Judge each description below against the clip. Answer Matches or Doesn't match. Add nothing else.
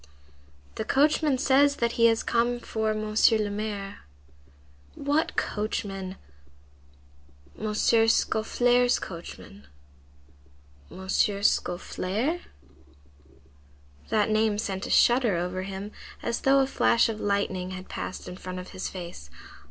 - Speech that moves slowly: Matches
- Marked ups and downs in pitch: Doesn't match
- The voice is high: Matches